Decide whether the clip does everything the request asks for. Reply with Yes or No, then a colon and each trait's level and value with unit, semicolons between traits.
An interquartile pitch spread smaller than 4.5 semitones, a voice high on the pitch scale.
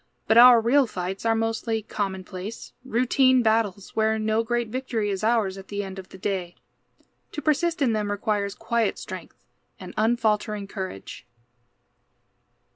Yes: average, 2.9 semitones; high, 220 Hz